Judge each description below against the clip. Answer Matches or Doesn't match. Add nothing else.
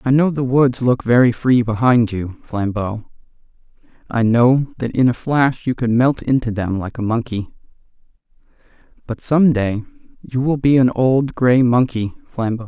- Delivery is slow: Doesn't match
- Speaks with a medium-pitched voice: Doesn't match